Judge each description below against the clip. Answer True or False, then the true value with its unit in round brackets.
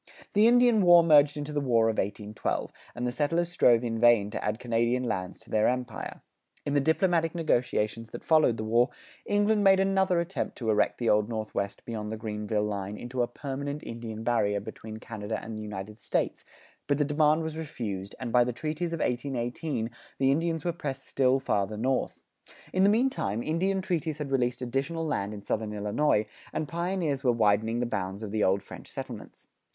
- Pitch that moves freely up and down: True (6.4 semitones)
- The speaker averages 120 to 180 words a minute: False (190 wpm)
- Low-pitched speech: True (125 Hz)